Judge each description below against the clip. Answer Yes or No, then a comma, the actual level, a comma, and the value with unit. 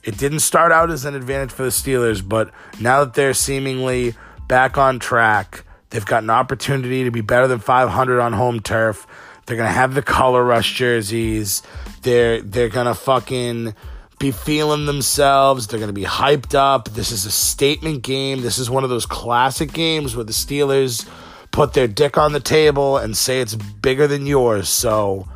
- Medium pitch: No, low, 125 Hz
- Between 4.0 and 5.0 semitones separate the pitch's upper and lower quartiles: No, average, 3.2 semitones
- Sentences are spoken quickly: No, average, 190 wpm